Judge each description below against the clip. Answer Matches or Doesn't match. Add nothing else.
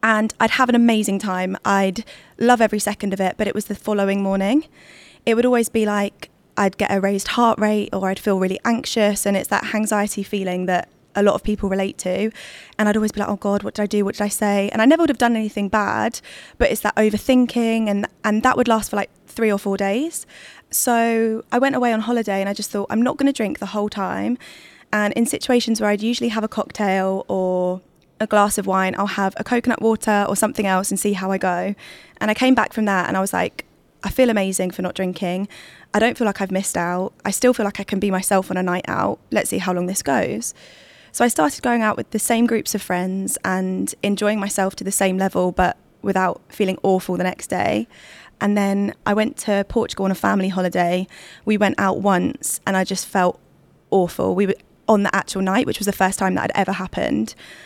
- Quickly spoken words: Matches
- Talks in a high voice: Matches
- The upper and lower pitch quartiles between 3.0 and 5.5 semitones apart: Doesn't match